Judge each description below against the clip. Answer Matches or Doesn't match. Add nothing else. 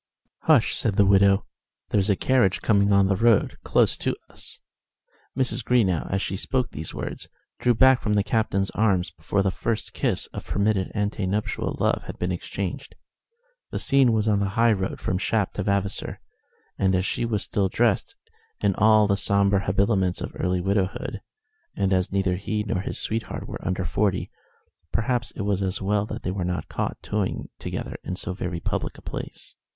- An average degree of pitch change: Doesn't match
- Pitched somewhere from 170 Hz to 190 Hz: Doesn't match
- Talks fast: Doesn't match